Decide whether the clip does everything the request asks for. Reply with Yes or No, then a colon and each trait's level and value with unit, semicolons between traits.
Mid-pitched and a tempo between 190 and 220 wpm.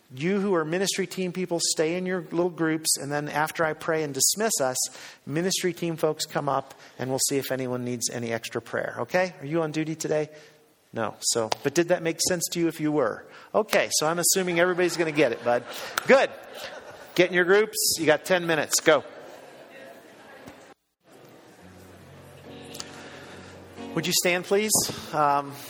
No: medium, 160 Hz; average, 175 wpm